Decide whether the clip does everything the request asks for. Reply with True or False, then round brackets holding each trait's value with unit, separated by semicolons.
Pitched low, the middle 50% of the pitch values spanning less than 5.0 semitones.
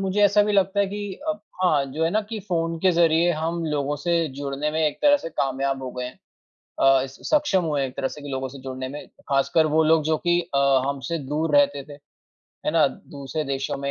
False (155 Hz; 3.9 semitones)